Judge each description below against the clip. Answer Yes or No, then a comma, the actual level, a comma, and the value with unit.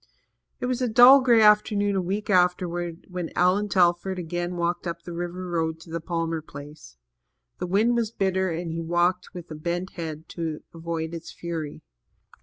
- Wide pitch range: No, narrow, 2.4 semitones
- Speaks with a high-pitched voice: No, medium, 175 Hz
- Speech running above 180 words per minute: No, average, 175 wpm